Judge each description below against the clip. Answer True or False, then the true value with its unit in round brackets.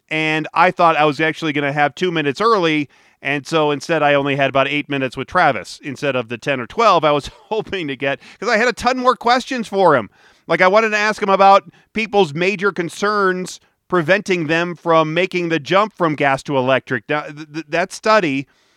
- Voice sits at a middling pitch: True (165 Hz)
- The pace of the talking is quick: True (215 wpm)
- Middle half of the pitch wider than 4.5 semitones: True (5.1 semitones)